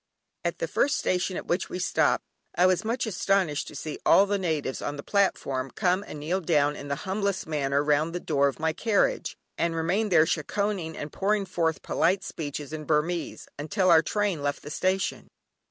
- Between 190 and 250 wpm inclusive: Yes, average, 195 wpm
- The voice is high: No, medium, 170 Hz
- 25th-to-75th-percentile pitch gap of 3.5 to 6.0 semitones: Yes, average, 4.5 semitones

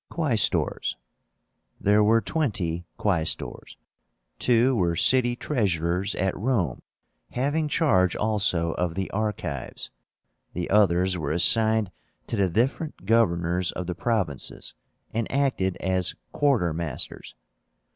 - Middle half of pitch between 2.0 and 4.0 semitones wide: No, average, 4.9 semitones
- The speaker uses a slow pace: Yes, slow, 105 wpm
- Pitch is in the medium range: No, very low, 95 Hz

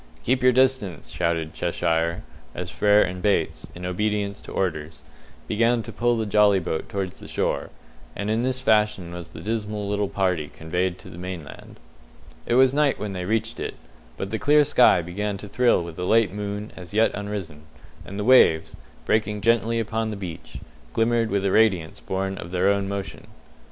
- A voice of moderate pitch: No, low, 100 Hz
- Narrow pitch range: No, average, 3.6 semitones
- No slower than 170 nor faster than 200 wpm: Yes, average, 185 wpm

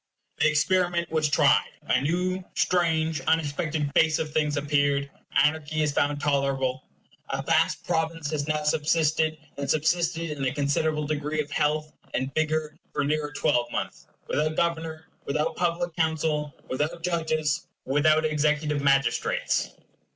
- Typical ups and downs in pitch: No, narrow, 1.7 semitones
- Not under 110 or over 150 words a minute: Yes, slow, 135 wpm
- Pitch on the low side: No, medium, 155 Hz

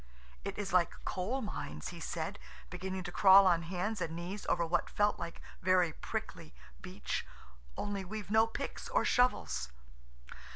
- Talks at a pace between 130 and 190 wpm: Yes, average, 155 wpm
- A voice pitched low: No, medium, 185 Hz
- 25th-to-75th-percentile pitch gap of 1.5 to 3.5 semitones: Yes, average, 3.1 semitones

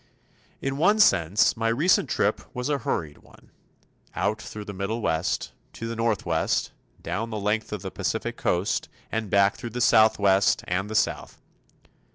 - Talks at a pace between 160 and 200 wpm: Yes, average, 165 wpm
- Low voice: Yes, low, 110 Hz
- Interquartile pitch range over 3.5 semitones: No, average, 2.9 semitones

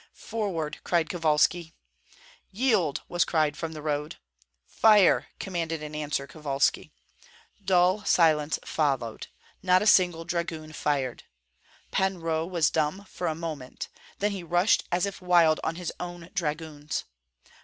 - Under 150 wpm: Yes, slow, 135 wpm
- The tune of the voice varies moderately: Yes, average, 3.0 semitones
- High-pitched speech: No, medium, 165 Hz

